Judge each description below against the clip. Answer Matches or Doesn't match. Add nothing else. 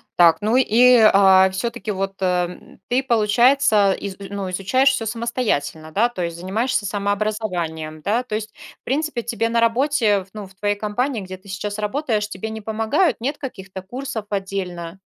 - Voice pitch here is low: Doesn't match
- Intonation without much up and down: Doesn't match